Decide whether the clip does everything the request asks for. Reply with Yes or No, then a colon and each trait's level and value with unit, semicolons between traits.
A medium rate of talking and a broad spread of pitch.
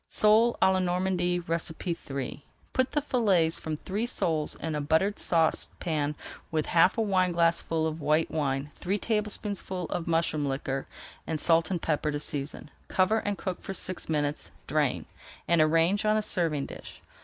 No: average, 160 wpm; average, 3.7 semitones